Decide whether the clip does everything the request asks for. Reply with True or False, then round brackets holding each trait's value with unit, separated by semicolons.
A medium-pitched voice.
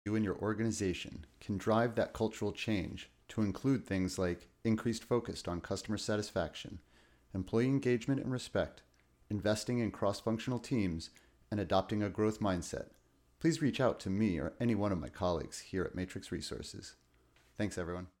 False (105 Hz)